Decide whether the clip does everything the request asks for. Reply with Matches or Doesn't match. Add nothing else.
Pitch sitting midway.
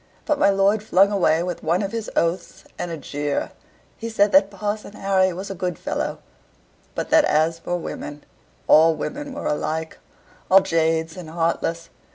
Matches